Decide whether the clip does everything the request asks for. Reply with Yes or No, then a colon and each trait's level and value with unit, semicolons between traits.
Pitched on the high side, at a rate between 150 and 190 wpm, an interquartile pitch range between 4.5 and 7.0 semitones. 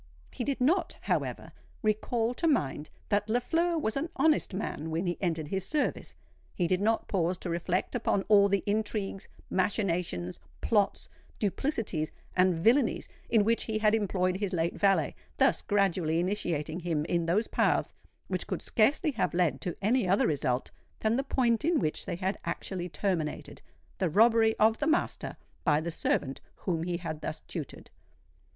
Yes: high, 195 Hz; average, 160 wpm; average, 4.8 semitones